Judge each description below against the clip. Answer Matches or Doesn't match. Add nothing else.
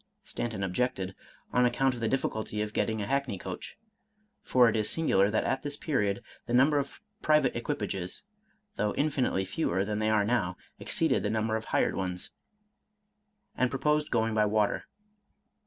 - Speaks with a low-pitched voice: Matches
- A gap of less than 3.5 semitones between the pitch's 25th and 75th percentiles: Doesn't match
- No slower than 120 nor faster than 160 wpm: Doesn't match